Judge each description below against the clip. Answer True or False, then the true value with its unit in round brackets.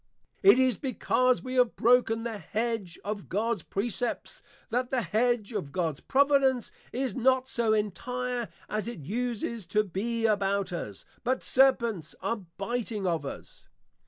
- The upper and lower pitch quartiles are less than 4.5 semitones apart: True (3.7 semitones)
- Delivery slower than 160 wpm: True (150 wpm)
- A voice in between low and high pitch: False (230 Hz)